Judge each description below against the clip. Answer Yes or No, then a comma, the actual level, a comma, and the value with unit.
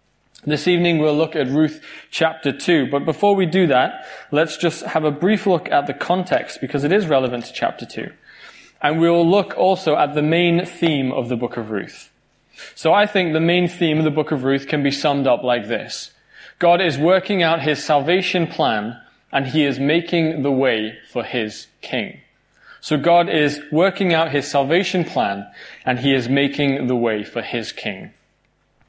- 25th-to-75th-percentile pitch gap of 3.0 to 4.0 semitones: Yes, average, 3.7 semitones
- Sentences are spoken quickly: No, average, 190 wpm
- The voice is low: No, medium, 155 Hz